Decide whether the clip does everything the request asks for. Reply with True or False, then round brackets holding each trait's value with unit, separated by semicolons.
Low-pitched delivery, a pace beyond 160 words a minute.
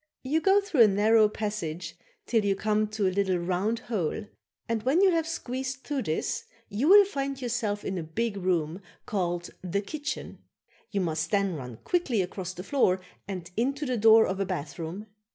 False (210 Hz; 185 wpm)